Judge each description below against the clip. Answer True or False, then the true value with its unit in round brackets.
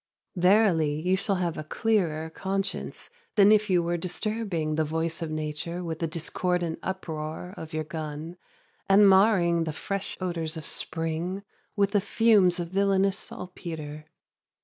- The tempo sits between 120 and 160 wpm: True (150 wpm)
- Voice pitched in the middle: True (175 Hz)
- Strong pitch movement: False (3.5 semitones)